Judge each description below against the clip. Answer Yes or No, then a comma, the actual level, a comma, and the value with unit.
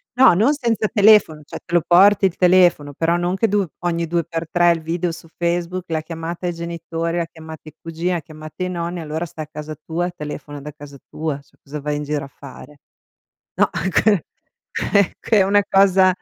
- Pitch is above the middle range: No, medium, 170 Hz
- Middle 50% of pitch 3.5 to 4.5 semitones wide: No, average, 2.7 semitones